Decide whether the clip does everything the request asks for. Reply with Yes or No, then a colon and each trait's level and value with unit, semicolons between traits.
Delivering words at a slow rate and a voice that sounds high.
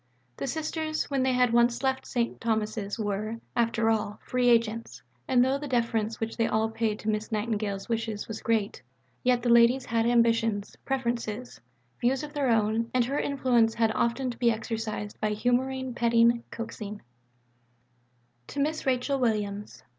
No: average, 160 wpm; high, 230 Hz